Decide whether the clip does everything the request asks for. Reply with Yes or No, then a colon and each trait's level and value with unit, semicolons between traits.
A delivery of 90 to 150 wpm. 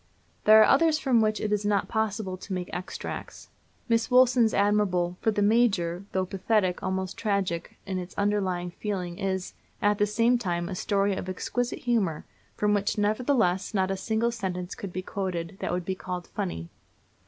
No: average, 175 wpm